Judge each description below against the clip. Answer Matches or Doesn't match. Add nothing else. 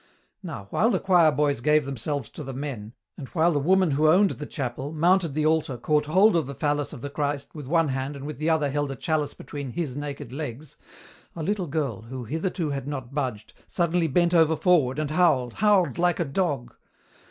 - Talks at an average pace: Doesn't match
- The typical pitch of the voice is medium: Matches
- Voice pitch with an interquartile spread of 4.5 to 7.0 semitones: Doesn't match